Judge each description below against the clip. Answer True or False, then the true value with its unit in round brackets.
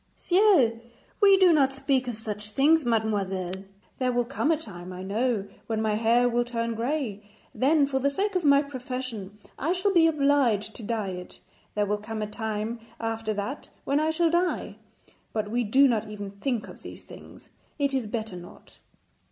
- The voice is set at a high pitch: True (235 Hz)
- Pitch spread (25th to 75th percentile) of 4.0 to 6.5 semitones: True (4.9 semitones)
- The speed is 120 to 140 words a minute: False (185 wpm)